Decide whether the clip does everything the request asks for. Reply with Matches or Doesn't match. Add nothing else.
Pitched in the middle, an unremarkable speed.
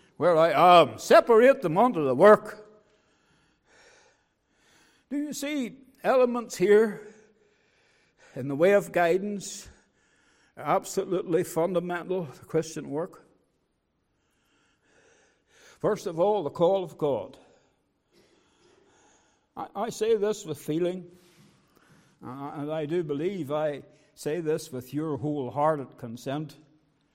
Doesn't match